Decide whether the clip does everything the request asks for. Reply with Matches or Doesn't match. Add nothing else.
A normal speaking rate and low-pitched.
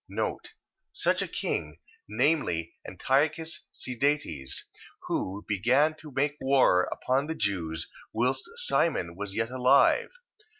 Doesn't match